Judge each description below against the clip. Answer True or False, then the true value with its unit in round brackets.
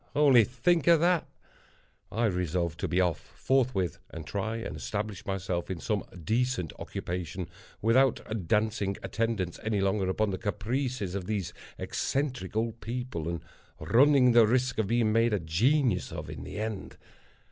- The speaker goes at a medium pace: True (155 wpm)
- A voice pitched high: False (110 Hz)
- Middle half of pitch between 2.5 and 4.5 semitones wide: False (4.9 semitones)